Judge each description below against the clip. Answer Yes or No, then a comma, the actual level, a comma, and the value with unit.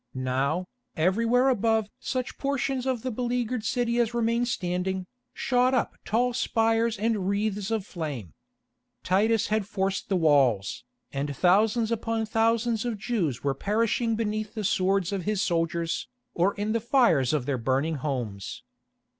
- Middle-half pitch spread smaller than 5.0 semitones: No, wide, 5.4 semitones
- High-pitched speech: Yes, high, 210 Hz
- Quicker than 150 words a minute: No, average, 145 wpm